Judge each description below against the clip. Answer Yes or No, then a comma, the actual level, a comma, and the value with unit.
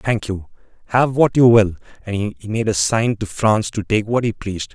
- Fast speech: Yes, fast, 255 wpm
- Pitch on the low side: Yes, low, 105 Hz